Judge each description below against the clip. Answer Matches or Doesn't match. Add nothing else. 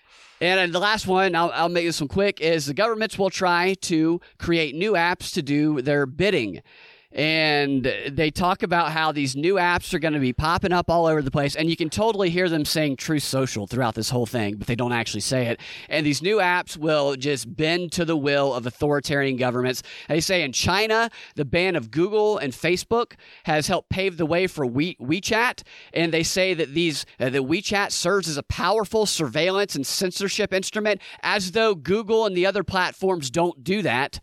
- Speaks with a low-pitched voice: Doesn't match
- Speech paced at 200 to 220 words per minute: Matches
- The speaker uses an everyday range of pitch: Matches